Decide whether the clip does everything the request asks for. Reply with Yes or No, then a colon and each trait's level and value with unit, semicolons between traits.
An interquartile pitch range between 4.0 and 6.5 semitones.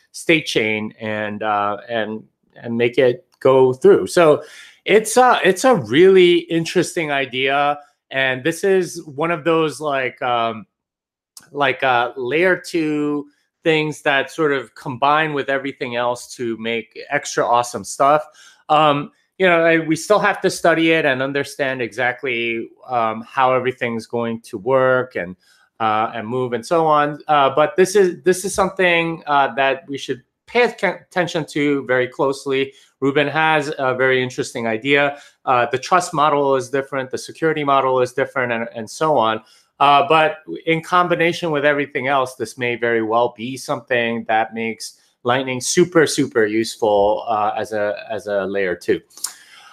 Yes: average, 5.1 semitones